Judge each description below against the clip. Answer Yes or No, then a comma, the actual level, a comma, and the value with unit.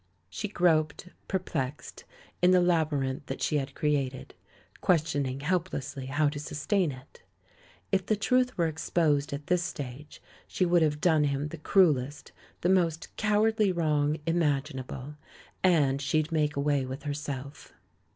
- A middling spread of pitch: Yes, average, 3.7 semitones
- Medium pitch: Yes, medium, 150 Hz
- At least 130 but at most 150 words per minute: Yes, average, 140 wpm